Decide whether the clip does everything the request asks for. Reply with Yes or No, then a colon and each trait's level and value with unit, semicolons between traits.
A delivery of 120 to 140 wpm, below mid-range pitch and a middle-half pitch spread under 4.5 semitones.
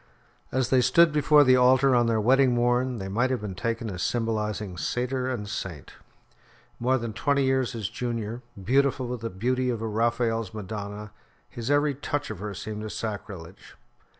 No: average, 175 wpm; low, 120 Hz; average, 3.3 semitones